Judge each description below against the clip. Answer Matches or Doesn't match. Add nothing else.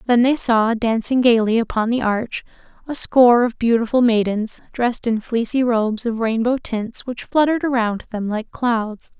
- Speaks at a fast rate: Doesn't match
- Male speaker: Doesn't match